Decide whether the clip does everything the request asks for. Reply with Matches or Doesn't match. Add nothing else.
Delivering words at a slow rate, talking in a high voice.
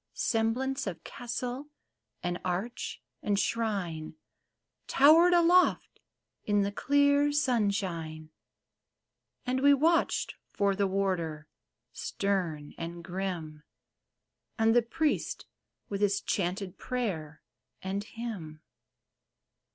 Matches